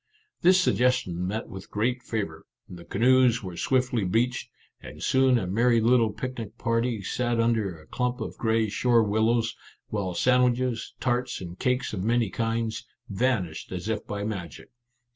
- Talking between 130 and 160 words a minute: Yes, average, 155 wpm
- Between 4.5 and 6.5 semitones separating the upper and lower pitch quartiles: No, average, 3.6 semitones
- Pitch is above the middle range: No, low, 115 Hz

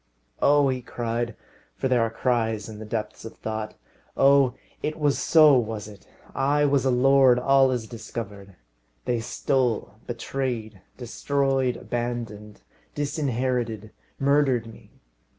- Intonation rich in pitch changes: No, average, 3.4 semitones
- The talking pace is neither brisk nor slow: No, slow, 130 wpm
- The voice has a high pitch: No, low, 120 Hz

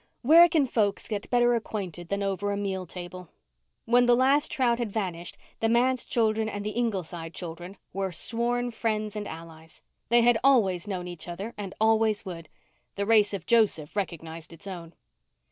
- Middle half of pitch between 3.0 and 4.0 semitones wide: No, average, 4.8 semitones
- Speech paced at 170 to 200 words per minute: Yes, average, 175 wpm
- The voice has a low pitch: No, high, 205 Hz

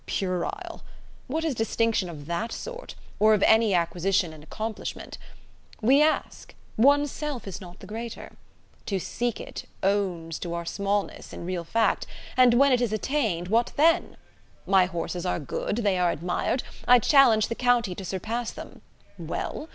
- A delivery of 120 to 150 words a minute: No, average, 160 wpm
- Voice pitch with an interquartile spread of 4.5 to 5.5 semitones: Yes, average, 5.2 semitones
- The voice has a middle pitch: No, high, 215 Hz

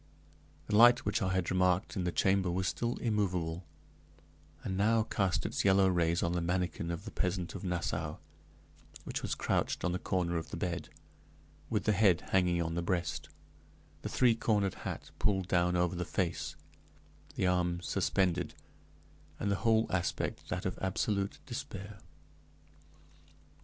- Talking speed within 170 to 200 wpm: No, average, 155 wpm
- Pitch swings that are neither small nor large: No, narrow, 2.3 semitones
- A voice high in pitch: No, very low, 90 Hz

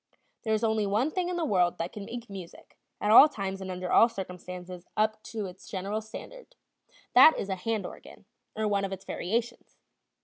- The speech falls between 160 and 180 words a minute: No, average, 200 wpm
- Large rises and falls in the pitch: No, average, 3.3 semitones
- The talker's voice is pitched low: No, high, 210 Hz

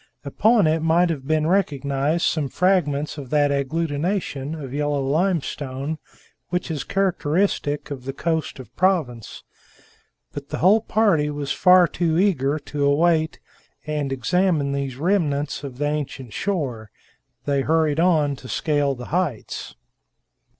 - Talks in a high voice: No, medium, 150 Hz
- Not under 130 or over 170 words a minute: Yes, slow, 135 wpm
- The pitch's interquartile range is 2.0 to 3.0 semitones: No, average, 3.5 semitones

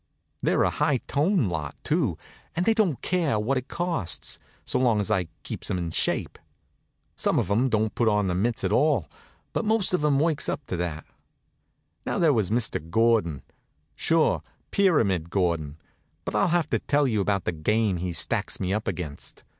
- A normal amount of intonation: No, wide, 8.6 semitones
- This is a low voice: Yes, low, 110 Hz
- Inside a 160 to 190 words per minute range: Yes, average, 185 wpm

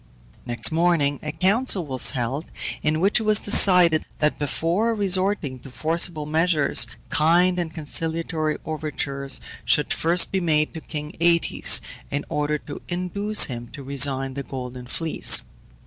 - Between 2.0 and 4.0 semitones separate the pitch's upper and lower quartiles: Yes, average, 3.7 semitones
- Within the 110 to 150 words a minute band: Yes, average, 145 wpm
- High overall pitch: No, medium, 155 Hz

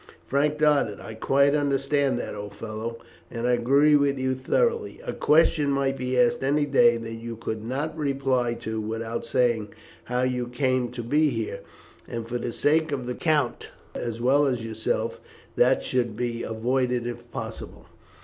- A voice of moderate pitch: No, low, 125 Hz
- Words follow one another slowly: No, average, 170 wpm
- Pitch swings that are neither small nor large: Yes, average, 3.2 semitones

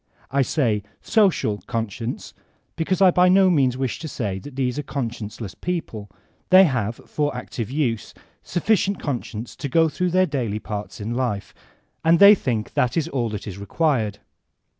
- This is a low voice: Yes, low, 130 Hz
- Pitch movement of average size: No, wide, 6.8 semitones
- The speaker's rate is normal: Yes, average, 165 wpm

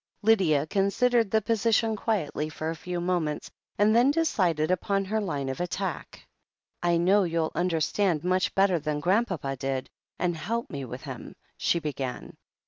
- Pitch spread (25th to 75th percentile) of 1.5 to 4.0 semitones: No, average, 4.9 semitones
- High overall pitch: No, medium, 180 Hz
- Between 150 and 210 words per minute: Yes, average, 160 wpm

